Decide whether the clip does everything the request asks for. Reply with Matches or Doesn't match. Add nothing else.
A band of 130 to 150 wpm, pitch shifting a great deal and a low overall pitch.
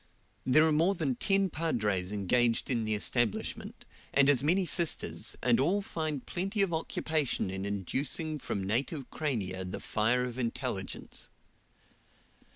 Matches